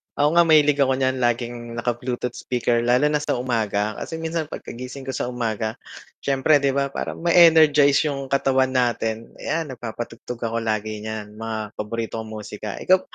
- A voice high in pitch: No, low, 125 Hz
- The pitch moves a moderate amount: Yes, average, 3.8 semitones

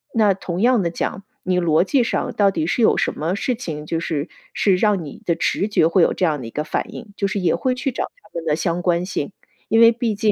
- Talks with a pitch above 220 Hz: No, medium, 185 Hz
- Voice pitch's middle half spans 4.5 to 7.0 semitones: Yes, average, 4.8 semitones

